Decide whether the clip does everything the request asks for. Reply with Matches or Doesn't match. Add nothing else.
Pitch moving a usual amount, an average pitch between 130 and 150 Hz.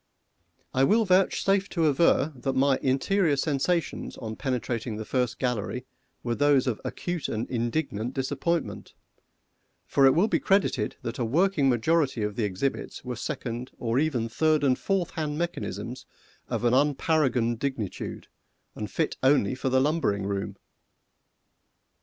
Matches